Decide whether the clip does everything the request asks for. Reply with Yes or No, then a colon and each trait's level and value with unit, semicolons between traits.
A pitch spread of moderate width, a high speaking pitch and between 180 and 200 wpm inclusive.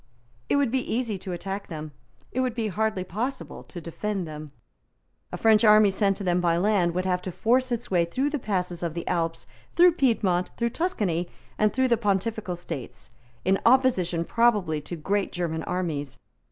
Yes: average, 4.8 semitones; high, 195 Hz; average, 185 wpm